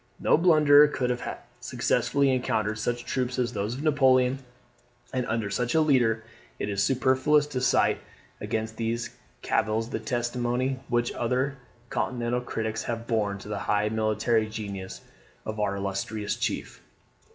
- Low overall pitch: Yes, low, 120 Hz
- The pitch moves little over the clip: No, average, 3.0 semitones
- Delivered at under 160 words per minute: Yes, average, 145 wpm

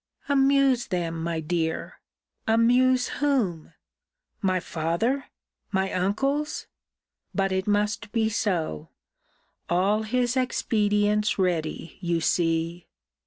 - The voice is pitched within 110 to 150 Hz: No, high, 205 Hz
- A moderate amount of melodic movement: No, wide, 5.9 semitones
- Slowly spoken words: Yes, slow, 95 wpm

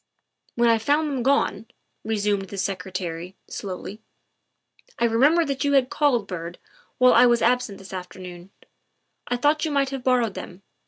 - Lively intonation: Yes, wide, 5.8 semitones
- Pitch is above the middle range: Yes, high, 230 Hz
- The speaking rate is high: No, average, 175 wpm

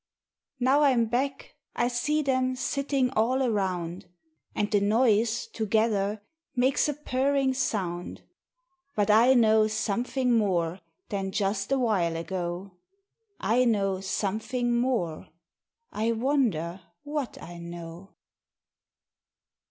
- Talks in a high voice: Yes, high, 220 Hz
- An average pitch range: Yes, average, 4.8 semitones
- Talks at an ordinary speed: No, slow, 105 wpm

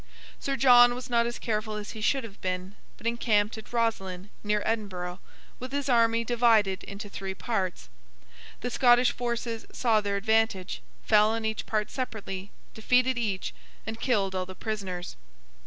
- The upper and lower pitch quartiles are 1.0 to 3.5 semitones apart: Yes, average, 3.1 semitones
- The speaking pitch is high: Yes, high, 220 Hz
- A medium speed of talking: Yes, average, 160 wpm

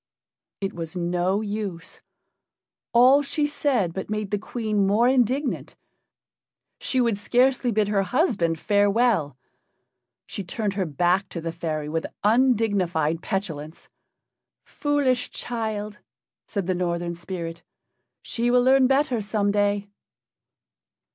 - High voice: Yes, high, 205 Hz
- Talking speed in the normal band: No, slow, 120 wpm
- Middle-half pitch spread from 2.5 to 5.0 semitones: No, wide, 5.5 semitones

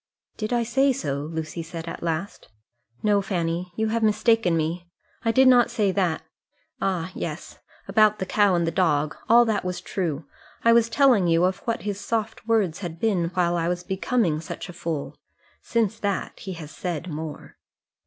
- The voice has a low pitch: No, medium, 185 Hz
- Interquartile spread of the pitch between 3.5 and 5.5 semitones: Yes, average, 4.8 semitones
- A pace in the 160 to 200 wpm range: Yes, average, 185 wpm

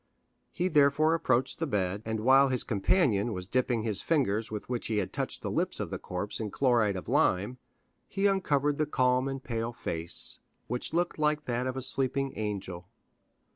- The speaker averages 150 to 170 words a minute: No, average, 185 wpm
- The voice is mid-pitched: No, low, 125 Hz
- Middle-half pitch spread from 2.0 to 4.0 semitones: No, average, 5.0 semitones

